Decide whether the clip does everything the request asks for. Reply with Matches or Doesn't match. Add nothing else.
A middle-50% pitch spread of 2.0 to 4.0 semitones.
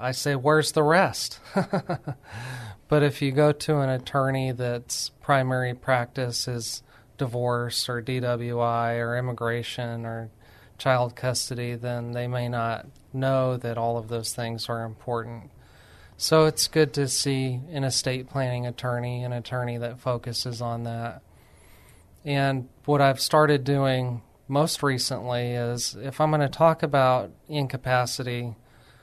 Matches